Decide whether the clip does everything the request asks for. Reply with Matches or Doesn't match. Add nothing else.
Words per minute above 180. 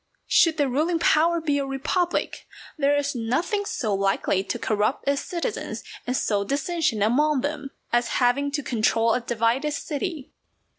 Doesn't match